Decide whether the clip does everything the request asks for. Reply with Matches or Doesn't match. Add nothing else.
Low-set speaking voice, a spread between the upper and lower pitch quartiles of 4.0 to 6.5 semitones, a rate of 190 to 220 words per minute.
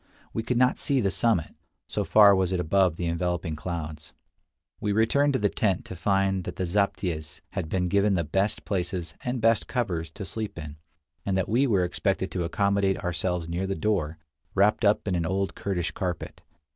Doesn't match